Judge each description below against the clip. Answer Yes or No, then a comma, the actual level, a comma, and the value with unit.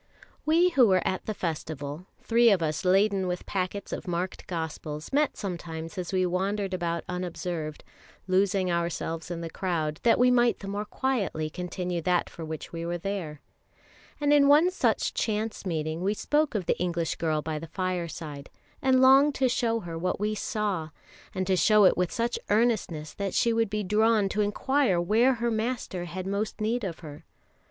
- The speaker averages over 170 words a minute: Yes, average, 185 wpm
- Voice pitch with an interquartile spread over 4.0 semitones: Yes, average, 4.6 semitones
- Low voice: No, medium, 185 Hz